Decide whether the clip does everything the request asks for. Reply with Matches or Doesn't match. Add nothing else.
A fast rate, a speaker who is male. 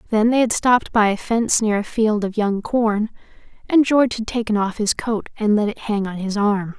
Doesn't match